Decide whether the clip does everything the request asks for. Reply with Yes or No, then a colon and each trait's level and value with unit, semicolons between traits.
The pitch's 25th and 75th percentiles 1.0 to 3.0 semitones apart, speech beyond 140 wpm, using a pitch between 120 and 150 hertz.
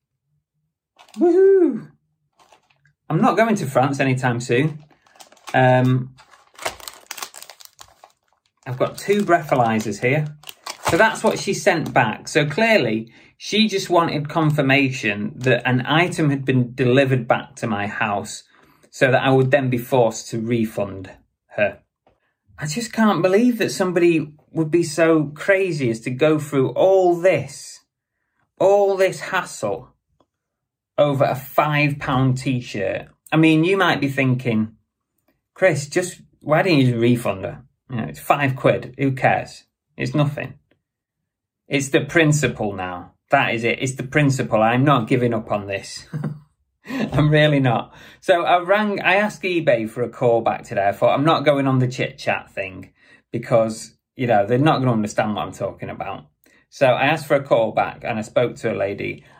No: average, 5.3 semitones; average, 160 wpm; medium, 140 Hz